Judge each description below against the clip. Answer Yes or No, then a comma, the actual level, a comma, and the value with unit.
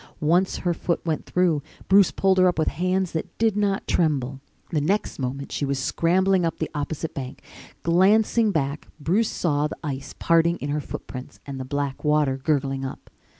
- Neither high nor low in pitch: Yes, medium, 160 Hz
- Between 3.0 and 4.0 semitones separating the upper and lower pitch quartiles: No, average, 4.5 semitones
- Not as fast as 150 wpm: No, average, 185 wpm